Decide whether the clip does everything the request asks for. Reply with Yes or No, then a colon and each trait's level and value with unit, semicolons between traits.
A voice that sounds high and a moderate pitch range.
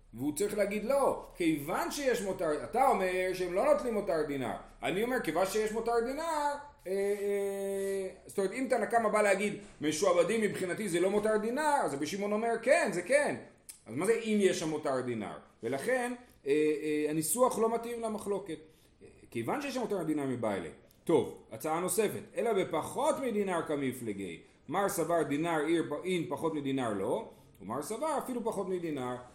No: high, 200 Hz; wide, 6.8 semitones